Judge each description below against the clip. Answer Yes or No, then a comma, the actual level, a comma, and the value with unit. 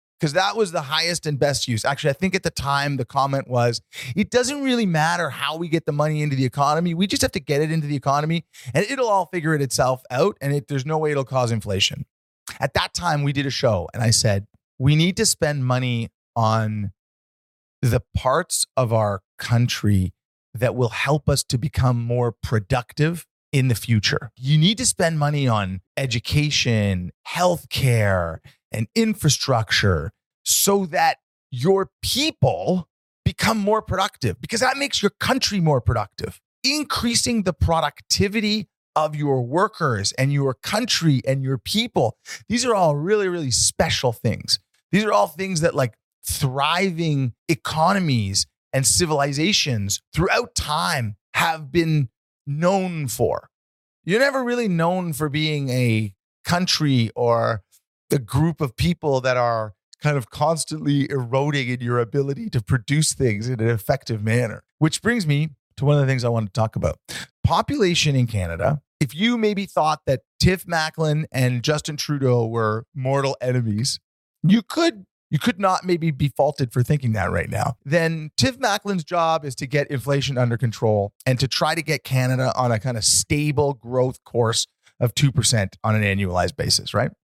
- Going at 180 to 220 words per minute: No, average, 170 wpm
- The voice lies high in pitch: No, medium, 140 Hz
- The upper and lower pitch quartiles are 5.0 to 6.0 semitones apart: Yes, wide, 5.5 semitones